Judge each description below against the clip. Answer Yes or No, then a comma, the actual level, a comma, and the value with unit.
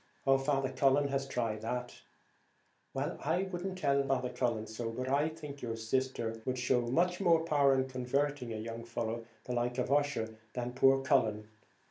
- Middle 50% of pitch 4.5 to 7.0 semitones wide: No, average, 3.1 semitones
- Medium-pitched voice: No, low, 130 Hz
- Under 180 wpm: Yes, average, 155 wpm